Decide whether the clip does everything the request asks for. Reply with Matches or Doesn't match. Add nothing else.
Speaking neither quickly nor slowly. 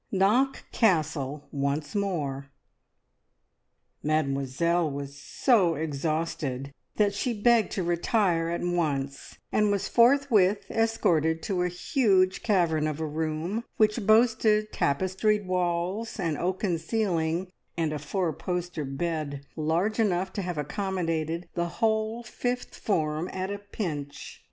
Doesn't match